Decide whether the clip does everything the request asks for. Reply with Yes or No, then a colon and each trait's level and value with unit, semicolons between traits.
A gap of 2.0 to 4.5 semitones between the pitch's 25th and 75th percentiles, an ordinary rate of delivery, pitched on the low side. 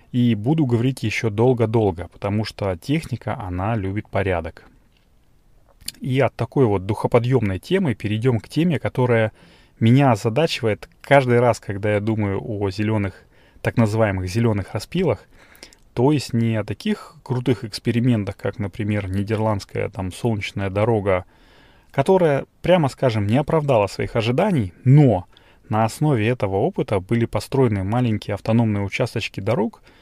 Yes: average, 3.7 semitones; average, 130 wpm; low, 115 Hz